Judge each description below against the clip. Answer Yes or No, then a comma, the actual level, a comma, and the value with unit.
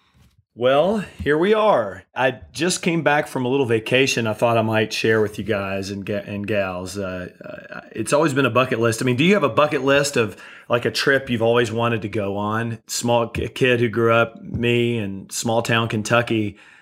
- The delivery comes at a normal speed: No, fast, 220 wpm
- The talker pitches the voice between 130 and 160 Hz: No, low, 115 Hz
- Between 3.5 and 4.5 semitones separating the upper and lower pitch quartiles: Yes, average, 3.8 semitones